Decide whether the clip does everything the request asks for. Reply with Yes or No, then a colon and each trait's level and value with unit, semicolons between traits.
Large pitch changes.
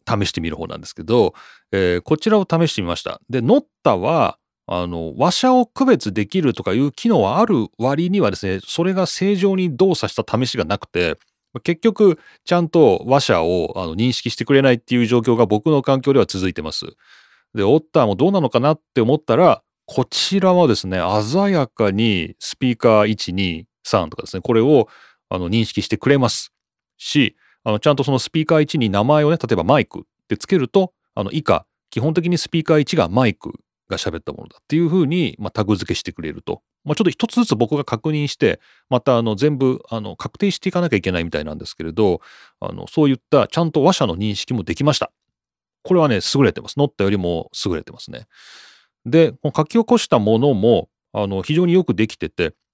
Yes: wide, 7.7 semitones